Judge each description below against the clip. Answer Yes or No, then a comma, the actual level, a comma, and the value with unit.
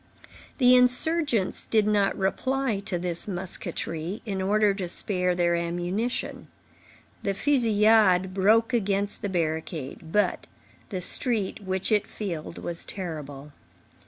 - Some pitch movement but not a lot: Yes, average, 3.6 semitones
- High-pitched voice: Yes, high, 195 Hz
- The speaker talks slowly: Yes, slow, 120 wpm